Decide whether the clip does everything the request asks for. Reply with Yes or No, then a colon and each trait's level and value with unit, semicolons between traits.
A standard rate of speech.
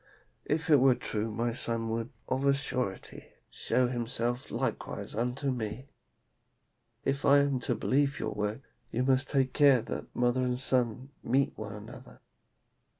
Yes: average, 150 wpm